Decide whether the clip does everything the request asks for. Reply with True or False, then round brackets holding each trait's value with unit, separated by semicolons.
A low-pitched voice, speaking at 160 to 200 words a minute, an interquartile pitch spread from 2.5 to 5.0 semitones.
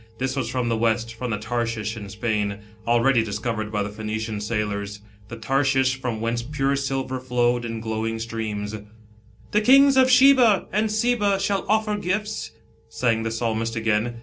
True (115 Hz; 175 wpm; 3.7 semitones)